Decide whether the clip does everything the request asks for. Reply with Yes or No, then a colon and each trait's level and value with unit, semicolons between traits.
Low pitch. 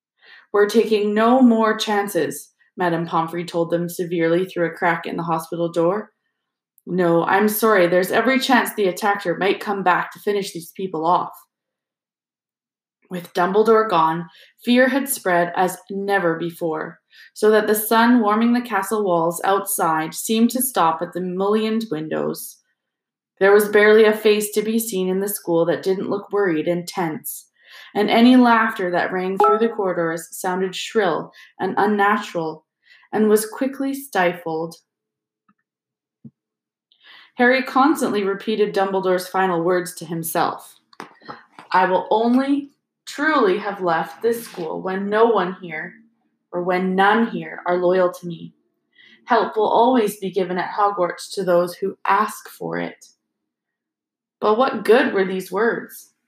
No: high, 195 Hz